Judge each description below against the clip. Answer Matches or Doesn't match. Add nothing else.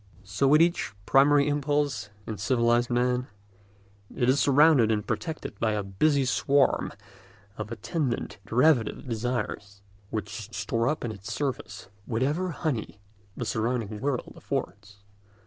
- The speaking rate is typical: Doesn't match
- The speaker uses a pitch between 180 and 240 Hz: Doesn't match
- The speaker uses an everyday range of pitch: Matches